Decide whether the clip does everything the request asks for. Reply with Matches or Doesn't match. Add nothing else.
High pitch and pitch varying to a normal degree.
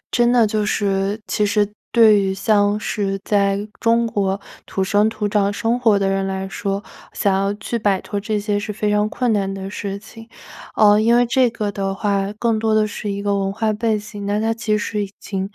Doesn't match